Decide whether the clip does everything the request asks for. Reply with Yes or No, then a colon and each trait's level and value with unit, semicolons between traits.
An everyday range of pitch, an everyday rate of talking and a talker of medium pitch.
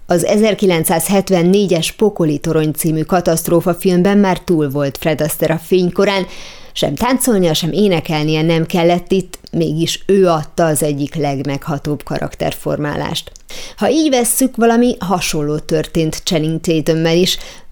Yes: average, 3.2 semitones; average, 120 wpm; medium, 170 Hz